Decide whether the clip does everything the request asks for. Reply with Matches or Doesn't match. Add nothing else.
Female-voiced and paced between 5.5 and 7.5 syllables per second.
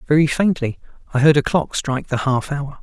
Doesn't match